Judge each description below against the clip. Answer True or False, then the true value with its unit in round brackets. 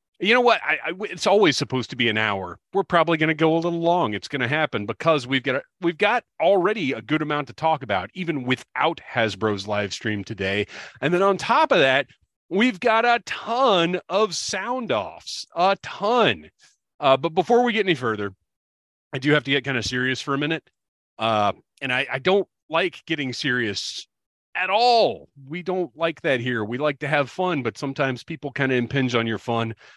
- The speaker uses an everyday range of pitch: False (6.9 semitones)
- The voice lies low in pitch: False (145 Hz)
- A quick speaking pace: True (210 wpm)